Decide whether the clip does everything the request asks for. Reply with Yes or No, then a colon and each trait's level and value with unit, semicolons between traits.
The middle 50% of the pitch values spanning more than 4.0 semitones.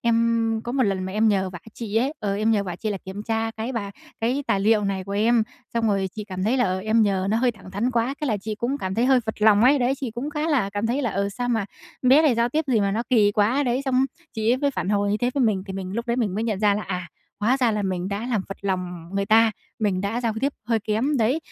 No: average, 3.4 semitones